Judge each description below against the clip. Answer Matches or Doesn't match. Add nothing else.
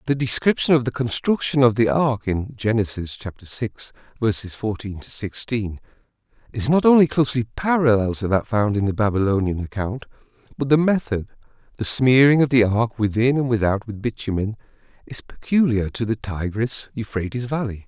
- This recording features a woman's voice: Doesn't match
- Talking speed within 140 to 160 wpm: Matches